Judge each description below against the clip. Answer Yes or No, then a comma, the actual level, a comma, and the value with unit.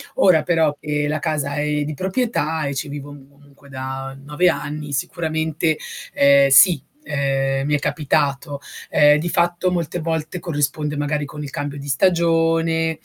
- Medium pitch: Yes, medium, 150 Hz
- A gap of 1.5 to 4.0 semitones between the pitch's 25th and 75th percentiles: Yes, narrow, 2.5 semitones